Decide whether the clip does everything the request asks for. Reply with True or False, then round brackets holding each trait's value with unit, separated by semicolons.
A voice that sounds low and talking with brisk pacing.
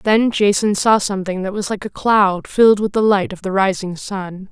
False (200 Hz; 225 wpm)